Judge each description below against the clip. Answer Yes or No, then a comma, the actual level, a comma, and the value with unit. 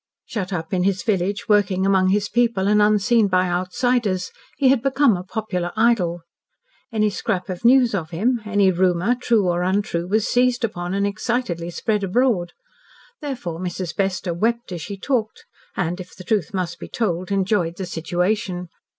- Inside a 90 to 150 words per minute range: No, average, 170 wpm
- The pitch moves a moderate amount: Yes, average, 3.9 semitones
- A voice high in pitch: Yes, high, 195 Hz